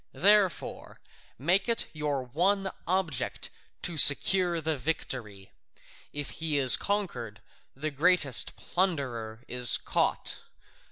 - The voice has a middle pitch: Yes, medium, 150 Hz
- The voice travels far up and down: Yes, wide, 6.2 semitones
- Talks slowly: Yes, slow, 105 wpm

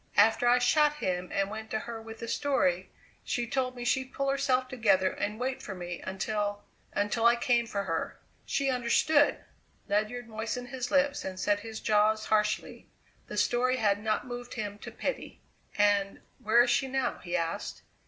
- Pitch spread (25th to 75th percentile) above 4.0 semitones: No, average, 3.5 semitones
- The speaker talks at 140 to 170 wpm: No, average, 180 wpm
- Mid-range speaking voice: No, high, 225 Hz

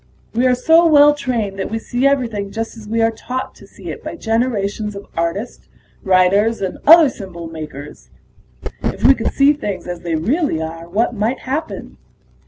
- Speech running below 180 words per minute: No, average, 185 wpm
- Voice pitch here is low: No, high, 225 Hz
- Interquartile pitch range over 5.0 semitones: Yes, wide, 5.4 semitones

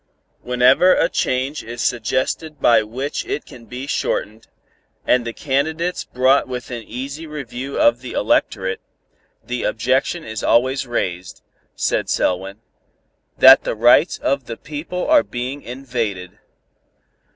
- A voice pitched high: No, low, 125 Hz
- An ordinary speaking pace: No, slow, 130 wpm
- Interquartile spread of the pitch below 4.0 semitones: Yes, average, 3.1 semitones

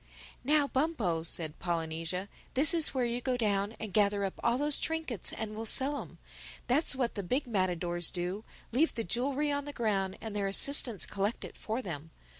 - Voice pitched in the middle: No, high, 220 Hz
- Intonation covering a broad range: Yes, wide, 5.9 semitones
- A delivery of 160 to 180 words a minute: No, average, 190 wpm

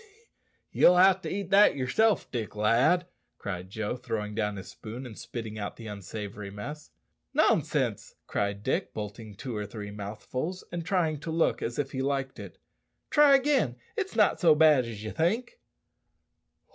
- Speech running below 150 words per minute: No, average, 165 wpm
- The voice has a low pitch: Yes, low, 125 Hz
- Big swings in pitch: Yes, wide, 8.7 semitones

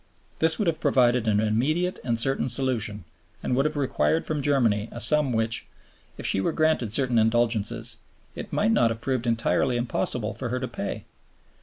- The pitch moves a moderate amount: Yes, average, 3.7 semitones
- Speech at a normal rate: Yes, average, 180 wpm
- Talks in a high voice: No, low, 120 Hz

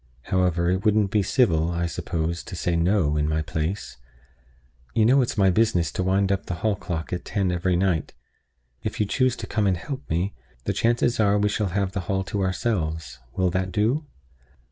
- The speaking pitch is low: Yes, very low, 95 Hz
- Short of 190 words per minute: No, fast, 205 wpm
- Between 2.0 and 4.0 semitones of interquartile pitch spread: Yes, average, 3.4 semitones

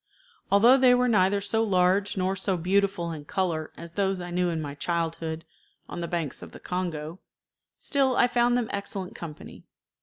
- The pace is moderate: Yes, average, 180 wpm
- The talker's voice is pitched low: No, medium, 185 Hz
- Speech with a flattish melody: No, average, 3.2 semitones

